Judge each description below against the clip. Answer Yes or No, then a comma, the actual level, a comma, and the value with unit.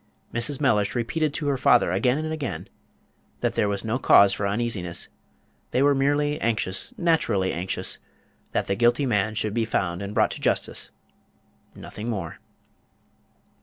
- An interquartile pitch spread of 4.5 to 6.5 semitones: Yes, wide, 5.6 semitones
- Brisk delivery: No, average, 155 wpm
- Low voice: Yes, low, 115 Hz